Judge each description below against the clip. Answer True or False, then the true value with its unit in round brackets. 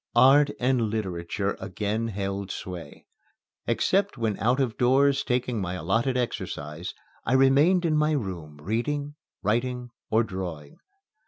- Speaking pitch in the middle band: False (115 Hz)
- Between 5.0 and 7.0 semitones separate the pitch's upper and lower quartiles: True (5.6 semitones)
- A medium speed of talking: False (130 wpm)